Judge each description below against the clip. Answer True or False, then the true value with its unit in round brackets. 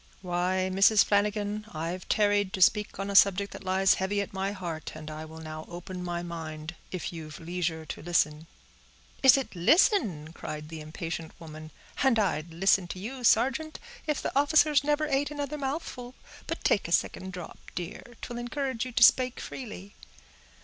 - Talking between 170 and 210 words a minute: True (175 wpm)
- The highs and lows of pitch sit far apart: True (6.4 semitones)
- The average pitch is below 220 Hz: True (190 Hz)